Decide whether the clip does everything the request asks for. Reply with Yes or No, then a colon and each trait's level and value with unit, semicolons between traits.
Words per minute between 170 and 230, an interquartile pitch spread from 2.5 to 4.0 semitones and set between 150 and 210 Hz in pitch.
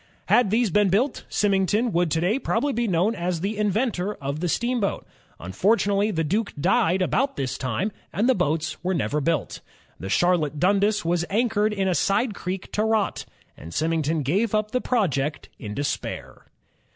No: average, 175 wpm; average, 4.8 semitones; high, 190 Hz